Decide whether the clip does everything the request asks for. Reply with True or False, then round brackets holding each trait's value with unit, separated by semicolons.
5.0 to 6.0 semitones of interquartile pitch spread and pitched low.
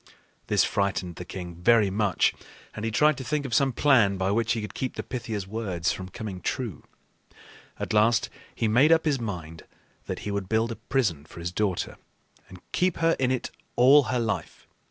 True (5.3 semitones; 110 Hz)